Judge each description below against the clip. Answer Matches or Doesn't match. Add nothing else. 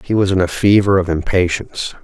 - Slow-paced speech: Doesn't match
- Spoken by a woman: Doesn't match